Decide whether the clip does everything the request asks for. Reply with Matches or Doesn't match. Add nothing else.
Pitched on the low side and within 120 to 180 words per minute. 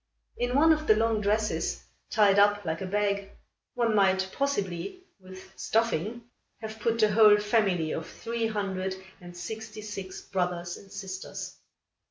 Doesn't match